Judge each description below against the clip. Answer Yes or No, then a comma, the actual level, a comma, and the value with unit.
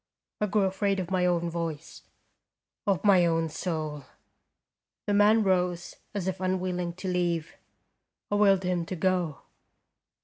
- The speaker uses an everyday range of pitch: No, narrow, 2.2 semitones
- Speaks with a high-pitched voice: No, medium, 180 Hz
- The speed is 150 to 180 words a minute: No, average, 140 wpm